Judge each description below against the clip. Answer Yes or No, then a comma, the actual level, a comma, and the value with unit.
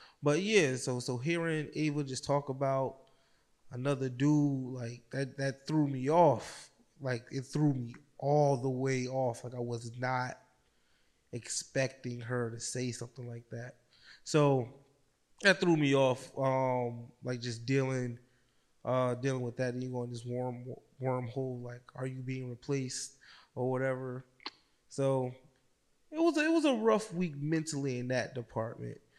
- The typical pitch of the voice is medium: No, low, 130 Hz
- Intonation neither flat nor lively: No, narrow, 2.2 semitones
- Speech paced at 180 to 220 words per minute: No, average, 150 wpm